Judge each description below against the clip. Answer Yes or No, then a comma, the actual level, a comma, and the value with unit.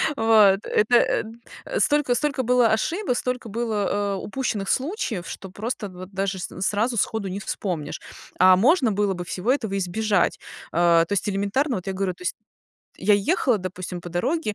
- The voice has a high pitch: Yes, high, 210 Hz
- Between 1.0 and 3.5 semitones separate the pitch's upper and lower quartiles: No, average, 4.4 semitones